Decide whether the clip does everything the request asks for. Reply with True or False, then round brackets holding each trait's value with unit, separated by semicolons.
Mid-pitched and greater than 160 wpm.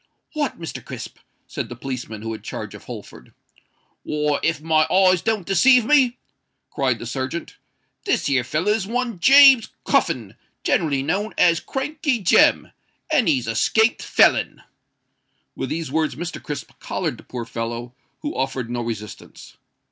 False (160 Hz; 150 wpm)